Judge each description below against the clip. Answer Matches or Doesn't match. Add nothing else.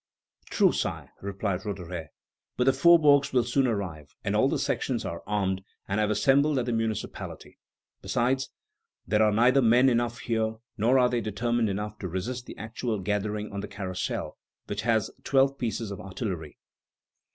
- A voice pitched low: Matches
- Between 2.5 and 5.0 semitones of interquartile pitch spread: Matches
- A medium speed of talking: Matches